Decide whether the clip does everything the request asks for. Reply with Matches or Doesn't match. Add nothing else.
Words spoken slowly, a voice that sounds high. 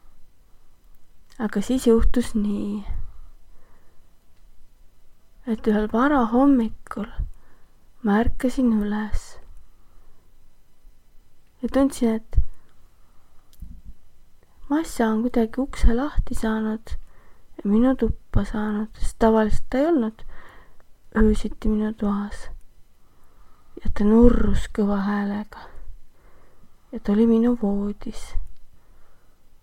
Matches